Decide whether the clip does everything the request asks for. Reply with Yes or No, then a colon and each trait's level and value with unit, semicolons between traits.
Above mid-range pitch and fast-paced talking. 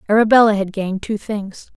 No: high, 205 Hz; average, 165 wpm